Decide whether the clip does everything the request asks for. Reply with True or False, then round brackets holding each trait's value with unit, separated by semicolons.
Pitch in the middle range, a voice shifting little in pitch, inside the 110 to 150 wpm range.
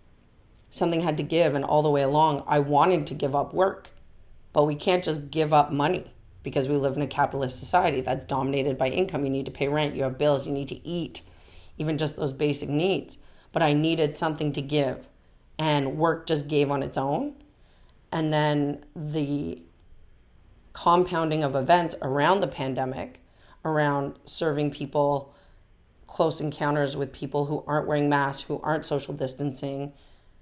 False (145 Hz; 2.2 semitones; 170 wpm)